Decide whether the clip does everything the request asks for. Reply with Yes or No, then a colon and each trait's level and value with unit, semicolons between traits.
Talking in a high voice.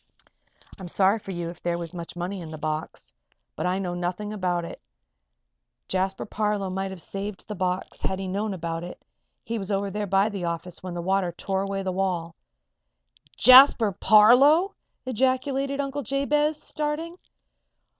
Yes: high, 195 Hz